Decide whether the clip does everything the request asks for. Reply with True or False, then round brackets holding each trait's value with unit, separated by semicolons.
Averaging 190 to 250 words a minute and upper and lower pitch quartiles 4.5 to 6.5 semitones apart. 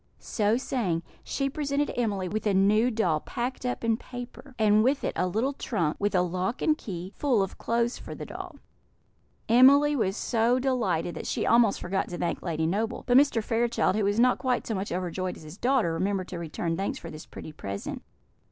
True (205 wpm; 5.3 semitones)